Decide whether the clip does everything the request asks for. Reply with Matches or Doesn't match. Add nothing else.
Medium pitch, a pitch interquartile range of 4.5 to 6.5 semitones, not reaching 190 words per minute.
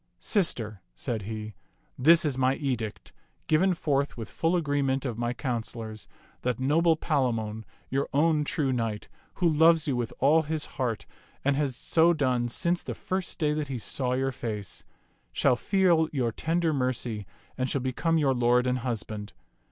Doesn't match